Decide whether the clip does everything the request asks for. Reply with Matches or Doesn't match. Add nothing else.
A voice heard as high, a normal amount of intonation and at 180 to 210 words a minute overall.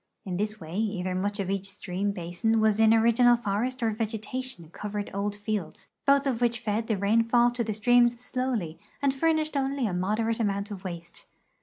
Matches